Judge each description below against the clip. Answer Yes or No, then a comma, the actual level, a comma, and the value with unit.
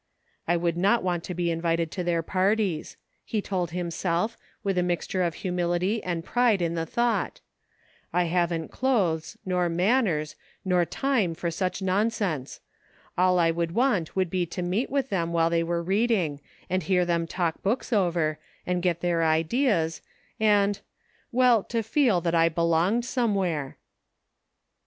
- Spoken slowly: No, average, 165 wpm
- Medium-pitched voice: Yes, medium, 180 Hz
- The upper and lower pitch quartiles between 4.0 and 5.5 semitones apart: No, average, 3.3 semitones